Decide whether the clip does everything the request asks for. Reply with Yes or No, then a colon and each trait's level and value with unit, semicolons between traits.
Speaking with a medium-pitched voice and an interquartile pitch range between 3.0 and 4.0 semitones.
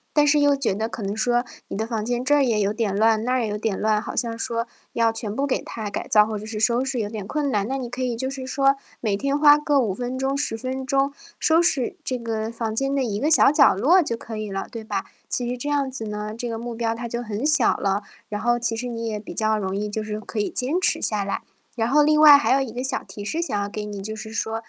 No: high, 230 Hz; average, 3.7 semitones